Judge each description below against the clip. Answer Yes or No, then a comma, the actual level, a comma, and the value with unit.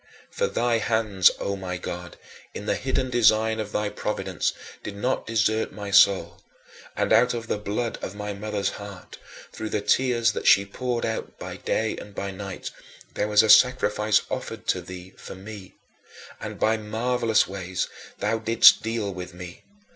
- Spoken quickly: No, average, 170 wpm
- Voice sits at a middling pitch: No, low, 105 Hz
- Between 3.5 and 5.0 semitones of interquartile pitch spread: No, narrow, 2.4 semitones